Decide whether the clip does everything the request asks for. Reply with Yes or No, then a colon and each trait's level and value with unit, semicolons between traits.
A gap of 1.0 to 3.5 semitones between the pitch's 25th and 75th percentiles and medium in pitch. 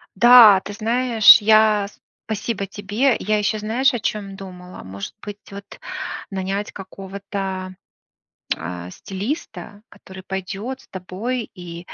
No: narrow, 2.6 semitones; high, 200 Hz